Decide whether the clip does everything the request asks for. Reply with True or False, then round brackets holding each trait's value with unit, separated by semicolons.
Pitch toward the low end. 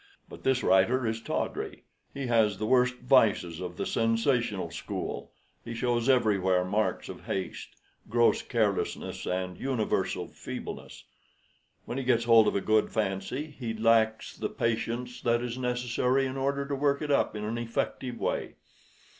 True (115 Hz)